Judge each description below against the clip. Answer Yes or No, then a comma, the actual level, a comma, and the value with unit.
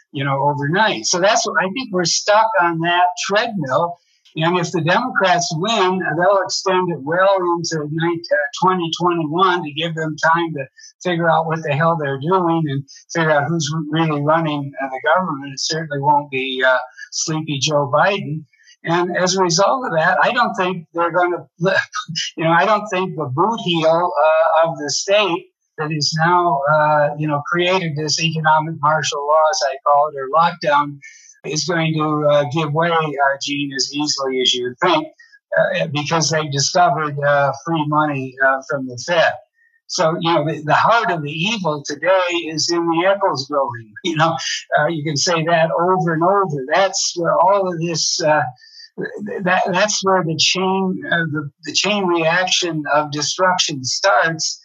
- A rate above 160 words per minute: Yes, average, 180 wpm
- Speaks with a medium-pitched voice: Yes, medium, 165 Hz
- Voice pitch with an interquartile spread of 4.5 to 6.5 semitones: No, average, 3.5 semitones